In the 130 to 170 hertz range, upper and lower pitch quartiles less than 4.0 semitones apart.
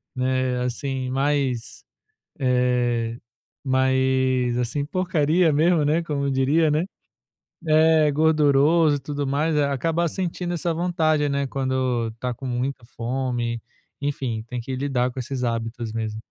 Yes: low, 135 Hz; average, 3.4 semitones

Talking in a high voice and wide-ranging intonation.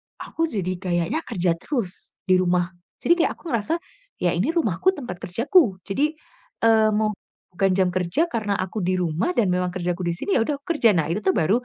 Yes: high, 195 Hz; wide, 6.1 semitones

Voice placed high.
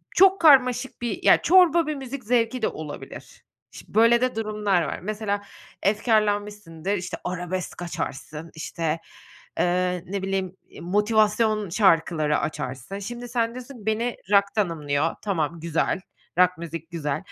Yes: high, 200 Hz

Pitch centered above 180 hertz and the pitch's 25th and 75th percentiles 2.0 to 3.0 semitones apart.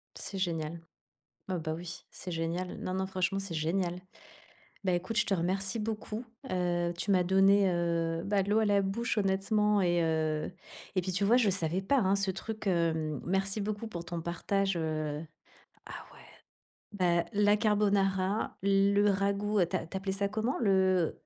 Yes: high, 190 Hz; average, 2.7 semitones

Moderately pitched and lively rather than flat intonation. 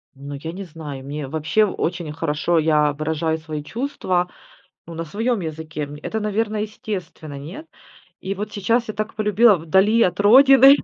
Yes: medium, 175 Hz; wide, 5.7 semitones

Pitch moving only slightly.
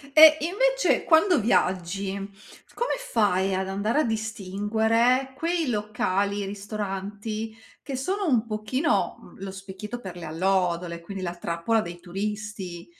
No: average, 4.1 semitones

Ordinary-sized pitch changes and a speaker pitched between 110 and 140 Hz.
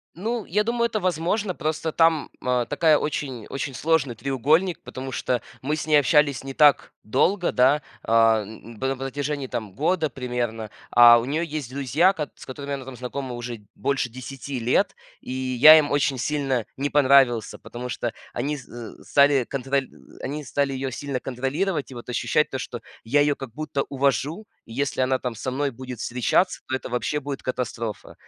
Yes: average, 3.1 semitones; low, 135 Hz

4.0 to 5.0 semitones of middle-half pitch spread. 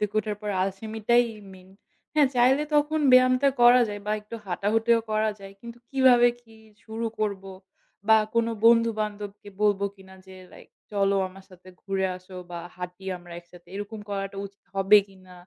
No: average, 3.2 semitones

